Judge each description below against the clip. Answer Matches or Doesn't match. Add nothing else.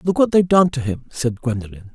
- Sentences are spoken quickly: Matches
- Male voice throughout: Matches